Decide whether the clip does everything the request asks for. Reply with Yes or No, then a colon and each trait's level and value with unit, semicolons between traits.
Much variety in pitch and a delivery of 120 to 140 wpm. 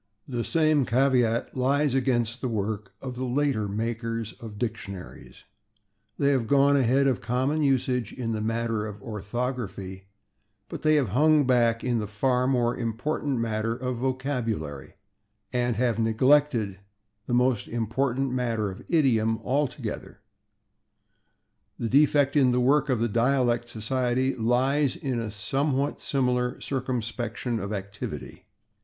No: average, 3.1 semitones; slow, 135 wpm